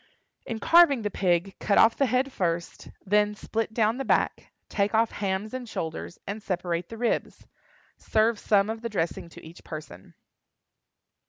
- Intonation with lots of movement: No, average, 4.2 semitones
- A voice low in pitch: No, high, 210 Hz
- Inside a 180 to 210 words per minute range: No, average, 165 wpm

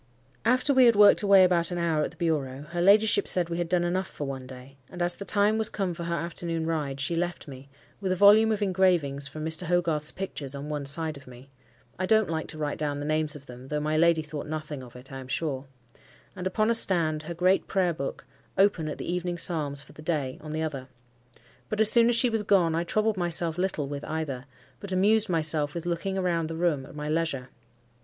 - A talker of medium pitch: Yes, medium, 165 Hz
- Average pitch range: Yes, average, 4.0 semitones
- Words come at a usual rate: No, fast, 240 wpm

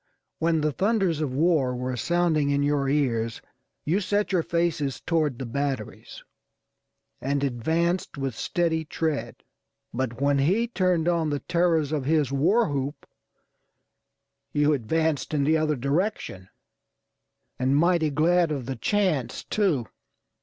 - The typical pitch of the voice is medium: Yes, medium, 150 Hz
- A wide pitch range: No, average, 3.8 semitones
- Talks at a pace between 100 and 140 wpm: Yes, slow, 135 wpm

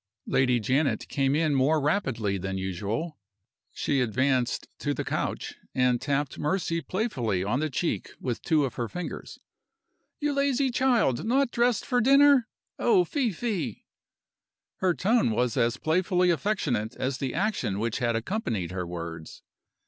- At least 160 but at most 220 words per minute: No, average, 150 wpm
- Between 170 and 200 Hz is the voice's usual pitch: No, medium, 140 Hz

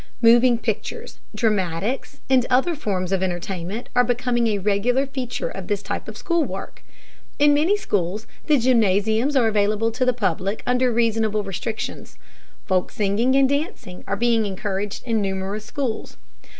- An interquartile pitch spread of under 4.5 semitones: Yes, average, 4.1 semitones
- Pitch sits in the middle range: No, high, 225 Hz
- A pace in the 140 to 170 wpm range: Yes, average, 150 wpm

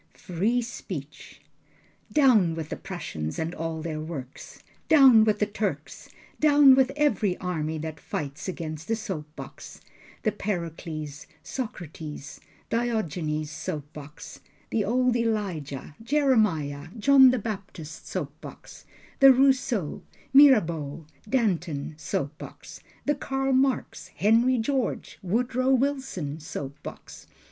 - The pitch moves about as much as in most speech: No, wide, 8.4 semitones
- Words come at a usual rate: No, slow, 120 wpm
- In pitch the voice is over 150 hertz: Yes, high, 190 Hz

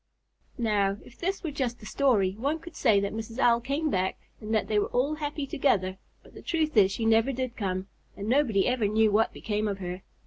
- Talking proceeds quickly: Yes, fast, 220 wpm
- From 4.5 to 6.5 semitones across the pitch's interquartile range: Yes, average, 5.2 semitones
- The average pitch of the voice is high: Yes, high, 225 Hz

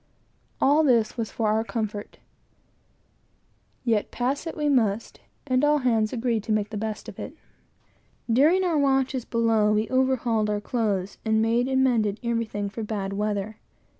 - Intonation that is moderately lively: Yes, average, 3.4 semitones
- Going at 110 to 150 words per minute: No, average, 160 wpm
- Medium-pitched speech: No, high, 225 Hz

